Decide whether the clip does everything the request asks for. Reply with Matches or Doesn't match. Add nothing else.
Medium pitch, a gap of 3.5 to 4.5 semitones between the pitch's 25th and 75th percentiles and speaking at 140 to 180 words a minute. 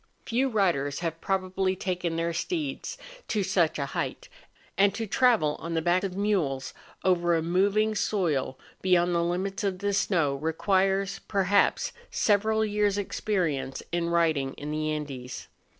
Matches